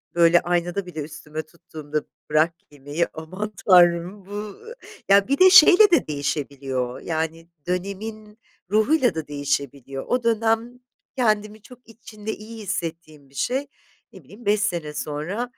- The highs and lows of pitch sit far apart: Yes, wide, 5.9 semitones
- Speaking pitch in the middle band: Yes, medium, 180 Hz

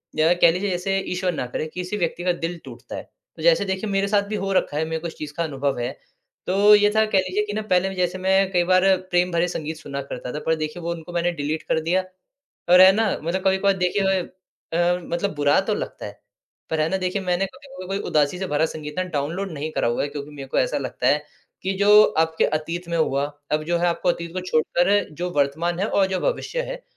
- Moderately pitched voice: Yes, medium, 175 Hz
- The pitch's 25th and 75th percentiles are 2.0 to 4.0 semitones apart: Yes, average, 3.5 semitones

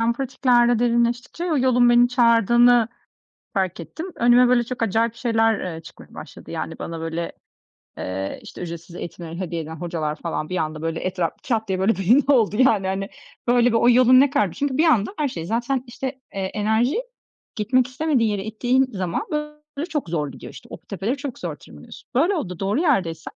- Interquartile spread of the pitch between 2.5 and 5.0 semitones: No, wide, 5.5 semitones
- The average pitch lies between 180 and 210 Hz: No, high, 230 Hz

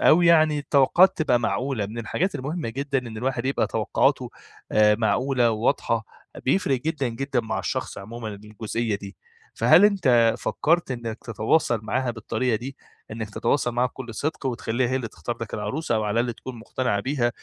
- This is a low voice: Yes, low, 120 Hz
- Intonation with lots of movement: No, average, 3.6 semitones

